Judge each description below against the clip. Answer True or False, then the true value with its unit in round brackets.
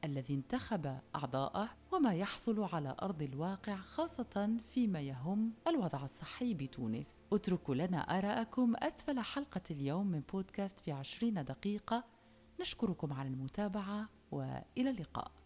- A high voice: True (195 Hz)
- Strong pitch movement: True (7.7 semitones)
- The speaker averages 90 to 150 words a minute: True (115 wpm)